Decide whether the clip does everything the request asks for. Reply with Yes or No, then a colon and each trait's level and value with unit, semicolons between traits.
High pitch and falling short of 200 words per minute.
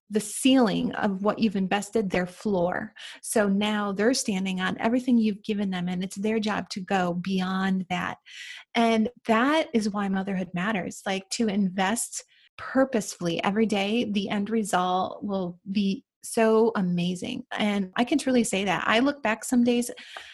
Yes: high, 210 Hz; average, 160 wpm